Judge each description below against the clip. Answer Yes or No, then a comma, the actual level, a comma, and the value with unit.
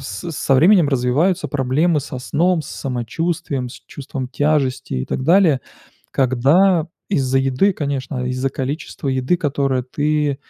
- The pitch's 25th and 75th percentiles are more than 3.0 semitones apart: Yes, average, 3.5 semitones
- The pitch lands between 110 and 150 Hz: Yes, medium, 140 Hz